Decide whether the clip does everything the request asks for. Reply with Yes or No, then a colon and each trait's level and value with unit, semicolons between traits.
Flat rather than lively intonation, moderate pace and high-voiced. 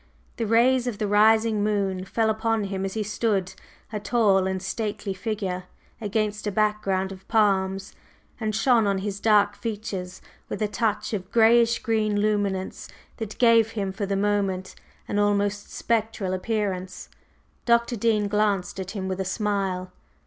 Yes: narrow, 2.3 semitones; average, 155 wpm; high, 205 Hz